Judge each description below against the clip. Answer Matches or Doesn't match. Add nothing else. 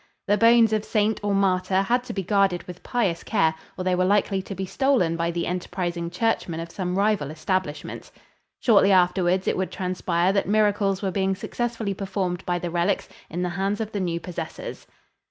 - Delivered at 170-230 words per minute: Matches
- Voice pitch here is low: Doesn't match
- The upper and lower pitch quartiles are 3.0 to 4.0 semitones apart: Doesn't match